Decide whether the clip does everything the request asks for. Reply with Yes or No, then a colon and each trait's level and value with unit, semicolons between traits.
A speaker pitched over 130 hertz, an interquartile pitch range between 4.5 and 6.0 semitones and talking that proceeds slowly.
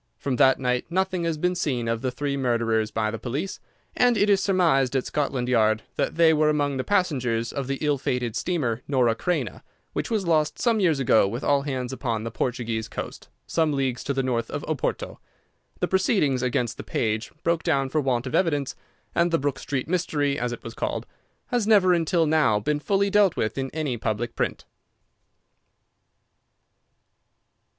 No: medium, 140 Hz; wide, 5.4 semitones; average, 185 wpm